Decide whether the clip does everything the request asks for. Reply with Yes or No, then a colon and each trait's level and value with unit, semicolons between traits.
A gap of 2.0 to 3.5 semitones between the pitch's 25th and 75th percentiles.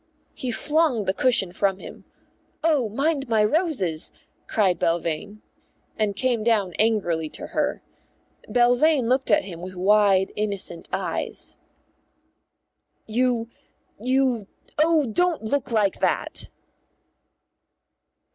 No: average, 4.9 semitones